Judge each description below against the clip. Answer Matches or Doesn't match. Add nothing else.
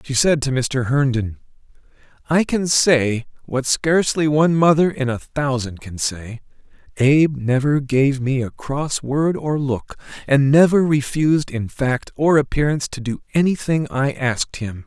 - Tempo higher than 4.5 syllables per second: Doesn't match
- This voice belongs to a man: Matches